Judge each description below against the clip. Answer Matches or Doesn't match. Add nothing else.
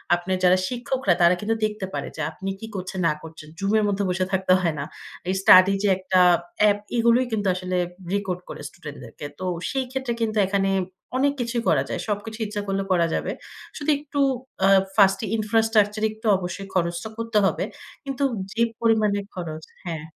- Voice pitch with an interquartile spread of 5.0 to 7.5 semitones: Doesn't match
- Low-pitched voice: Doesn't match